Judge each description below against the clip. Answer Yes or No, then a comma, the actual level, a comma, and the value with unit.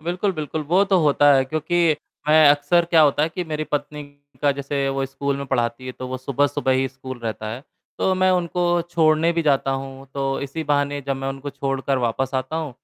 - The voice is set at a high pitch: No, medium, 145 Hz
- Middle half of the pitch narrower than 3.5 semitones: Yes, average, 2.8 semitones